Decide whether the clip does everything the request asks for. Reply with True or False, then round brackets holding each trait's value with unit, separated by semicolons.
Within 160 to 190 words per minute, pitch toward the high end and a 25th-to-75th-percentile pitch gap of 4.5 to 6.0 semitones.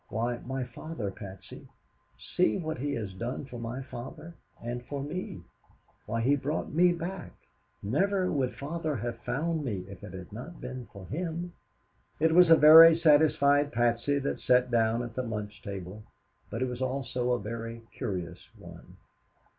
False (165 wpm; 125 Hz; 5.2 semitones)